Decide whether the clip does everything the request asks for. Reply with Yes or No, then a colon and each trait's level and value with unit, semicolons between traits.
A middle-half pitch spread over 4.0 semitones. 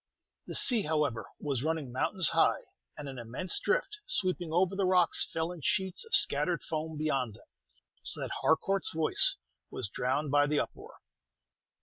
Yes: average, 4.7 semitones